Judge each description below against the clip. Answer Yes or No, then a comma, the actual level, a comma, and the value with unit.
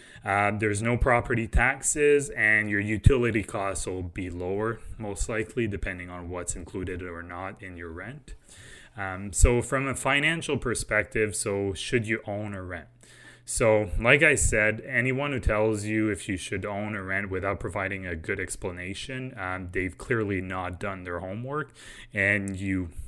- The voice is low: Yes, low, 100 Hz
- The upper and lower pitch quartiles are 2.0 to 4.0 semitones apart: Yes, average, 3.5 semitones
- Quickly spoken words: No, average, 165 wpm